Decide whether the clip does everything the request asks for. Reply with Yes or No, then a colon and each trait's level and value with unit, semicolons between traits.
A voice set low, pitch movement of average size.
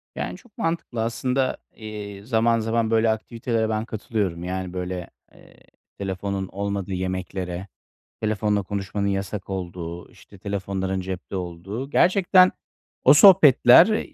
Yes: low, 100 Hz; average, 3.4 semitones